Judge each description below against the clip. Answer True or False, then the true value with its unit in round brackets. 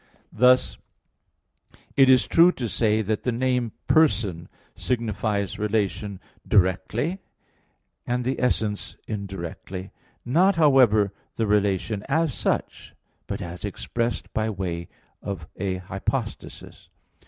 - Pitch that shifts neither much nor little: True (4.3 semitones)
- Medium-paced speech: False (110 wpm)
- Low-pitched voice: True (110 Hz)